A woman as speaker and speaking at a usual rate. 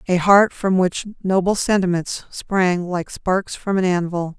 Yes: female; average, 165 wpm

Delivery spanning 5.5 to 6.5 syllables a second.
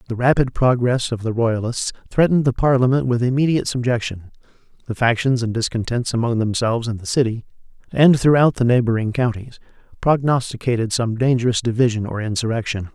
Yes: 5.9 syllables/s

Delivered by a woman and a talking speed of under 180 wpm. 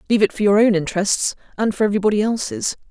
No: female; fast, 205 wpm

